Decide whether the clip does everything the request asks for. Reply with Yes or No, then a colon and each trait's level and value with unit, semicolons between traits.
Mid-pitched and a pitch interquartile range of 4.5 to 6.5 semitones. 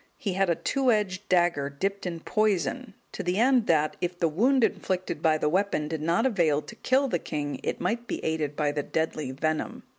Yes: medium, 175 Hz; average, 5.1 semitones